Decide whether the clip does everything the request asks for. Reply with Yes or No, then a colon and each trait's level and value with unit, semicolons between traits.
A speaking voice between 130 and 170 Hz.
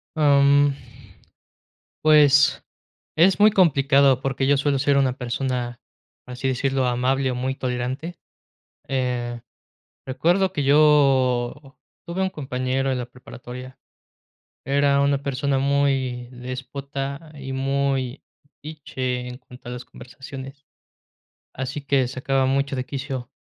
Yes: low, 135 Hz